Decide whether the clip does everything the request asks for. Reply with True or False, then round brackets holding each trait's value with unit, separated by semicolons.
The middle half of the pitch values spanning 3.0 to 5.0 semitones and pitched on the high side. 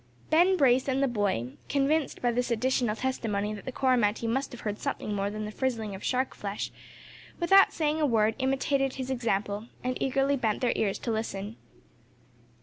True (4.1 semitones; 245 Hz)